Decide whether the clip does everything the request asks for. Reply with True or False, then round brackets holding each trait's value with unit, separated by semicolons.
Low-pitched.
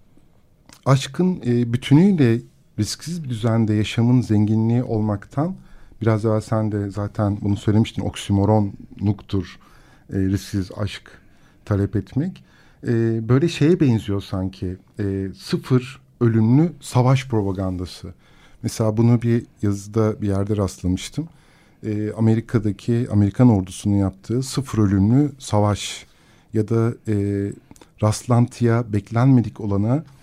True (110 Hz)